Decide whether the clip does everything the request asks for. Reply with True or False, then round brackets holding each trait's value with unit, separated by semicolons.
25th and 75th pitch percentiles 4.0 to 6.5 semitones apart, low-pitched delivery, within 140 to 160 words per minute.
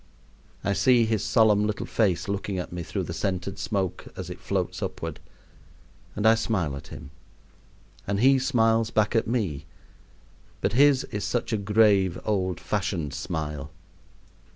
False (3.4 semitones; 105 Hz; 155 wpm)